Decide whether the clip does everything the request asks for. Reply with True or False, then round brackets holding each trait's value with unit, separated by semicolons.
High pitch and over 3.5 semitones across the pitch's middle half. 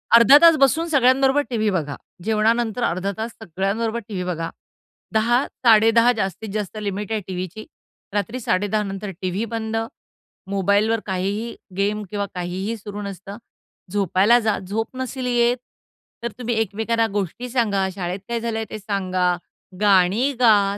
False (215 Hz; 3.1 semitones)